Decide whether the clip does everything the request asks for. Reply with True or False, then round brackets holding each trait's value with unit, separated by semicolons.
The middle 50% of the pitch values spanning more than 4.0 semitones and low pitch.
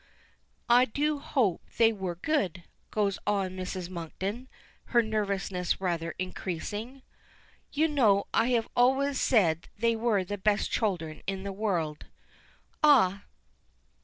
False (4.5 semitones; 205 Hz)